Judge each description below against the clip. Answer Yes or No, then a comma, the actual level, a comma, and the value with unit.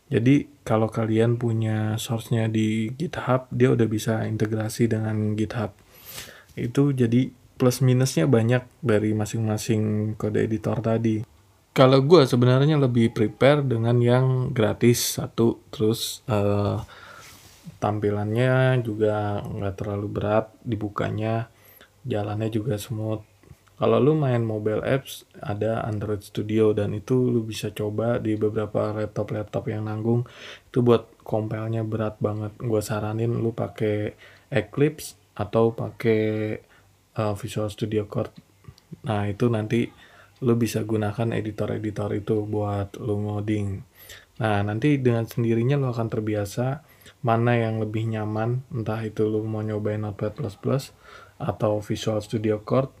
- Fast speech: No, average, 125 wpm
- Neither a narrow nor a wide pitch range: No, narrow, 2.2 semitones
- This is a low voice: Yes, low, 110 Hz